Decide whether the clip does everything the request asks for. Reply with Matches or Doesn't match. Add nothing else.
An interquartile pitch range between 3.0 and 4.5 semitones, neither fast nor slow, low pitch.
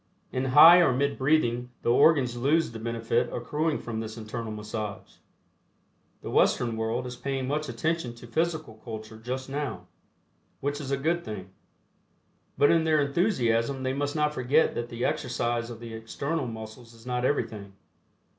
Matches